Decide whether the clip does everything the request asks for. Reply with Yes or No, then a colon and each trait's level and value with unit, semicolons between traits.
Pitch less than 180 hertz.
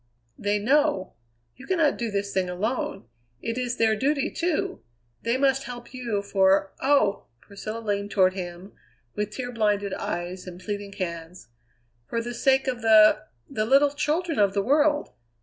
No: high, 215 Hz